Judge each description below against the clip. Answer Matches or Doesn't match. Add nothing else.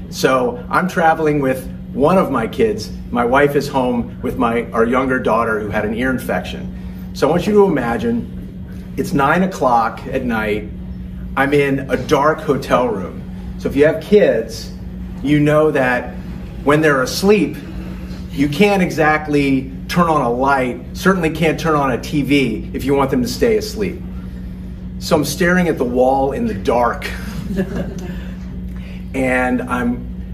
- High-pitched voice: Doesn't match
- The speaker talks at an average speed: Matches